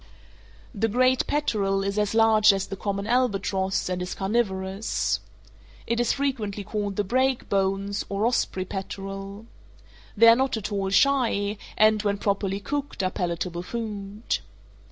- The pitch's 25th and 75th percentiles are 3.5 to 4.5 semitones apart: No, average, 2.8 semitones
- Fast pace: No, average, 145 wpm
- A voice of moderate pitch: No, high, 205 Hz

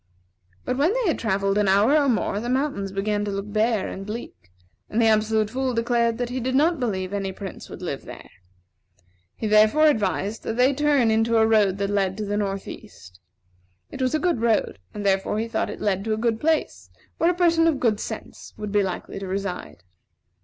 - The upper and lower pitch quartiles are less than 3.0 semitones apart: No, average, 4.2 semitones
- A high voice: Yes, high, 220 Hz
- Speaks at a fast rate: Yes, fast, 215 wpm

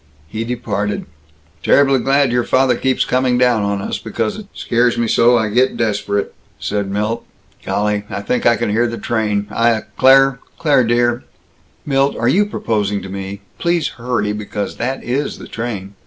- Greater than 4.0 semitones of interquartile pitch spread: No, average, 3.6 semitones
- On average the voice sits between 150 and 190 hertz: No, low, 120 Hz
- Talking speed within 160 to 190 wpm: Yes, average, 180 wpm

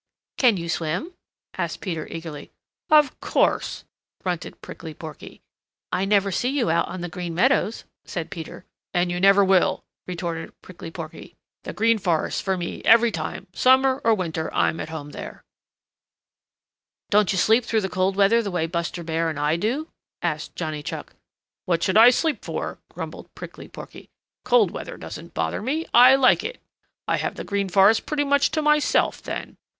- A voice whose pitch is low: No, high, 190 Hz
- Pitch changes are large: Yes, wide, 5.8 semitones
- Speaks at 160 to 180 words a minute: Yes, average, 175 wpm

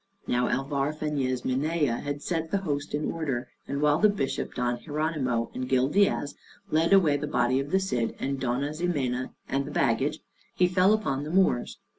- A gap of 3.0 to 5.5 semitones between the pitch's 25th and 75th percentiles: Yes, average, 3.8 semitones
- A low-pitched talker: No, medium, 145 Hz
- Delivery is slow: No, average, 185 wpm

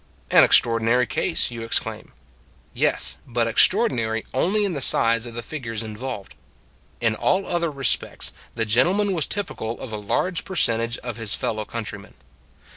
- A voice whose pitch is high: No, low, 120 Hz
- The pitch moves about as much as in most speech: No, wide, 6.3 semitones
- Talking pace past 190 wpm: No, average, 155 wpm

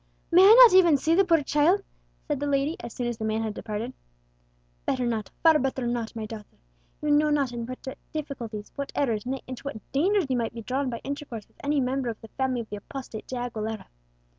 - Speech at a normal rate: No, fast, 225 wpm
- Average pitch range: Yes, average, 4.3 semitones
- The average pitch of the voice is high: Yes, very high, 260 Hz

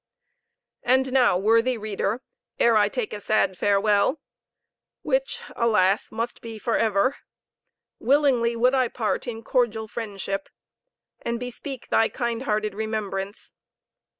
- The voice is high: Yes, high, 225 Hz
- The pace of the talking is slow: Yes, slow, 125 wpm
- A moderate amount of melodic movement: Yes, average, 3.0 semitones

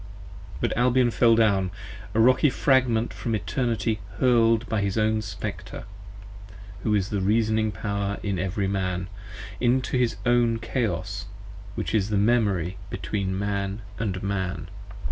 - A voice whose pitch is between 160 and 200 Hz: No, low, 110 Hz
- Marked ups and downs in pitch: No, average, 3.0 semitones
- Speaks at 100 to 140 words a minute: Yes, slow, 135 wpm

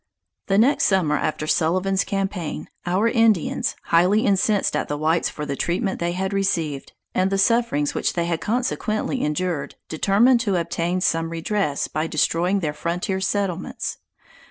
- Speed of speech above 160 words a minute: No, average, 155 wpm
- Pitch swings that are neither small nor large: Yes, average, 3.4 semitones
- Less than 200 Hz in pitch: Yes, medium, 185 Hz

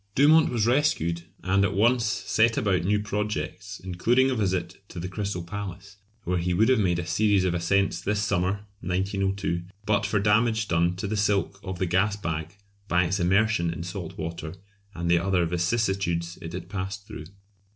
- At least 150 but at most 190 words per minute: Yes, average, 180 wpm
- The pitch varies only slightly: No, average, 3.2 semitones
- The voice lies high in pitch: No, very low, 95 Hz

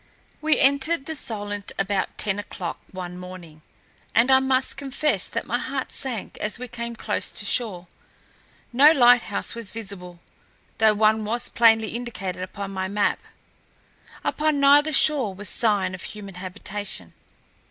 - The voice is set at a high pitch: Yes, high, 215 Hz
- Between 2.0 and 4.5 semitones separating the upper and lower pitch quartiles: No, average, 4.9 semitones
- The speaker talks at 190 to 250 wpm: No, average, 145 wpm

